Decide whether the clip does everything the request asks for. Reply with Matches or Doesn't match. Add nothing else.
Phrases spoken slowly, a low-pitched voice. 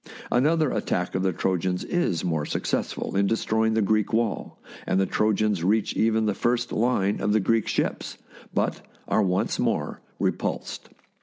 Doesn't match